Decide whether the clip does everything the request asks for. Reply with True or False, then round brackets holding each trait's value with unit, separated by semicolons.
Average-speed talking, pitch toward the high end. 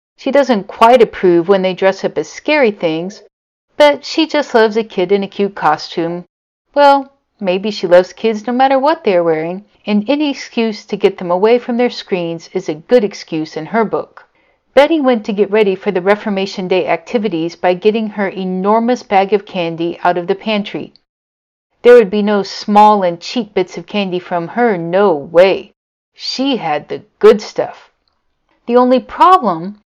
True (185 wpm; 205 Hz)